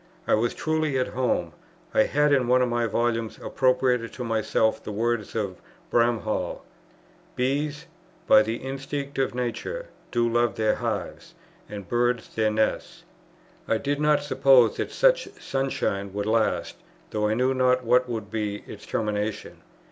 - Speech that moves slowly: No, average, 155 wpm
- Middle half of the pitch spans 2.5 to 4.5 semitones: Yes, average, 3.4 semitones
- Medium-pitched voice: No, low, 120 Hz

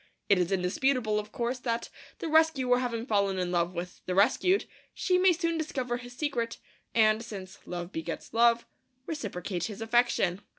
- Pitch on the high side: Yes, high, 230 Hz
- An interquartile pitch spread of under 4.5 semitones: No, average, 5.0 semitones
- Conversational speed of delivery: Yes, average, 165 wpm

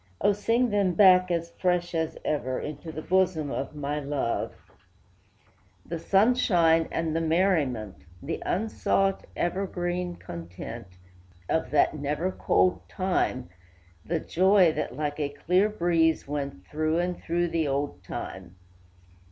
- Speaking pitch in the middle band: Yes, medium, 165 Hz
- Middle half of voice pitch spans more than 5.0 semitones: No, average, 4.1 semitones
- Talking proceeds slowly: Yes, slow, 130 wpm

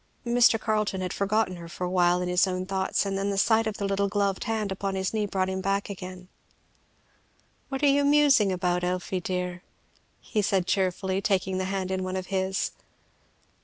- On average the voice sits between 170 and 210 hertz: Yes, high, 190 Hz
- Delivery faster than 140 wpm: Yes, average, 195 wpm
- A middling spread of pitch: No, narrow, 1.8 semitones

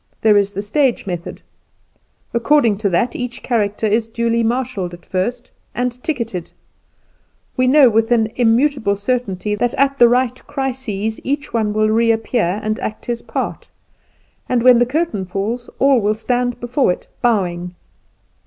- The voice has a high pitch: Yes, high, 230 Hz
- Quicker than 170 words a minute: No, average, 155 wpm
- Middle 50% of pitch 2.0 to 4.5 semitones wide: Yes, average, 3.2 semitones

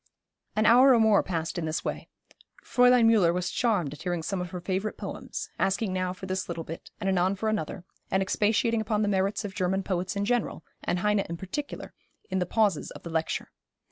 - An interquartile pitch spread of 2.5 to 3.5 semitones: Yes, average, 3.2 semitones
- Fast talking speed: Yes, fast, 210 wpm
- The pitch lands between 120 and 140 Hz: No, high, 190 Hz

